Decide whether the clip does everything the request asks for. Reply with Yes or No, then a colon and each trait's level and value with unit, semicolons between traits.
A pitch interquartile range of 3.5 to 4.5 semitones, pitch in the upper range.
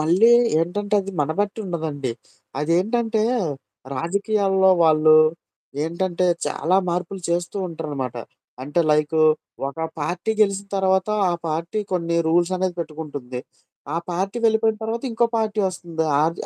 No: average, 3.8 semitones; medium, 175 Hz